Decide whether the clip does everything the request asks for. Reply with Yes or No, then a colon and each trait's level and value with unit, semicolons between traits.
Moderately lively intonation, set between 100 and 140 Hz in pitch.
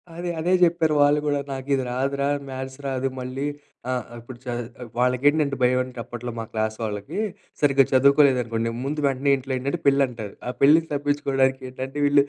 No: narrow, 2.1 semitones; low, 135 Hz